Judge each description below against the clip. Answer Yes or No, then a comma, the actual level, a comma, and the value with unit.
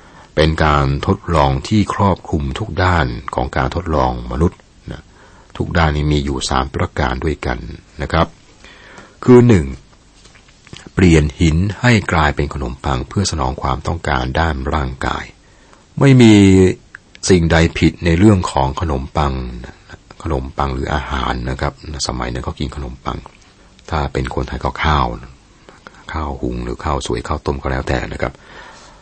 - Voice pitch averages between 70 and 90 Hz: Yes, very low, 75 Hz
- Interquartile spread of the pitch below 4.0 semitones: No, average, 4.7 semitones